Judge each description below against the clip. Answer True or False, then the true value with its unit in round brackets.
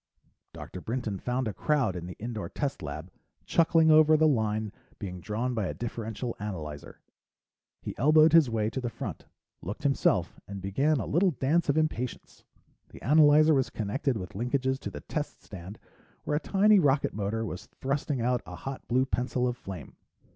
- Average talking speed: True (175 wpm)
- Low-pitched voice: True (125 Hz)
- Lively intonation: True (5.9 semitones)